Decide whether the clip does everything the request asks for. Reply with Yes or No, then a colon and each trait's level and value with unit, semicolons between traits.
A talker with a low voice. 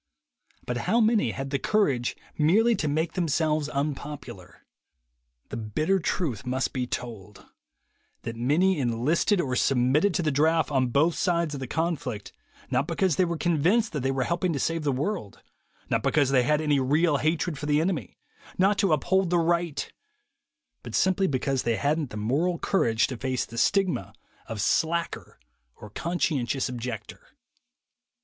No: medium, 150 Hz